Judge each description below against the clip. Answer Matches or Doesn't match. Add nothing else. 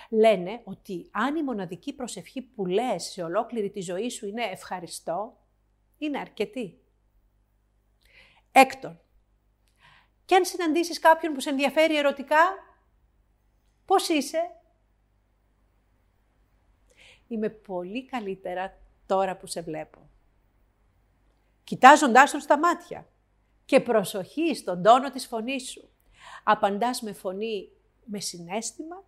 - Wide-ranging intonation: Matches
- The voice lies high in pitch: Matches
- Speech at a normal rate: Doesn't match